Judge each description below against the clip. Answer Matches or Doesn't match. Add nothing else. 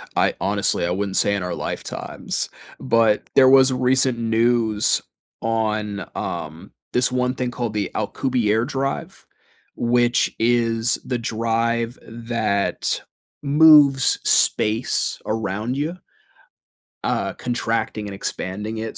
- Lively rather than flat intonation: Doesn't match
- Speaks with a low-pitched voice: Matches